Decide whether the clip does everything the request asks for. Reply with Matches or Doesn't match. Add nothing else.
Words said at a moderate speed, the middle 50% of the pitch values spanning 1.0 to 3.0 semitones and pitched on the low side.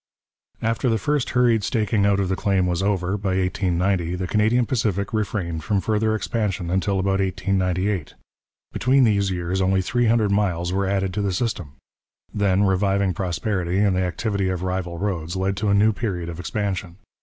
Matches